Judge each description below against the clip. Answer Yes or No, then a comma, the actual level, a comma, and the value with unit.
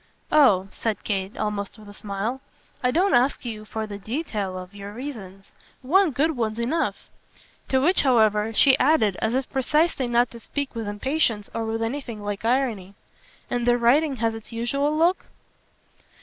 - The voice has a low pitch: No, high, 235 Hz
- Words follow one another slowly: No, average, 170 wpm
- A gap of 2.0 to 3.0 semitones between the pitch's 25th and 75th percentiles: No, average, 4.4 semitones